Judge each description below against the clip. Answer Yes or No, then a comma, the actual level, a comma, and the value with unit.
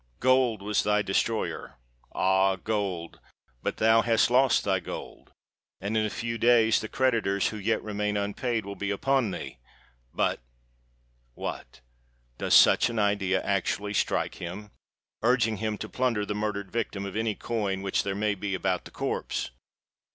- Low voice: Yes, low, 105 Hz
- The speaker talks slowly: No, average, 145 wpm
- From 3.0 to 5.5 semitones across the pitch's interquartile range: No, narrow, 2.4 semitones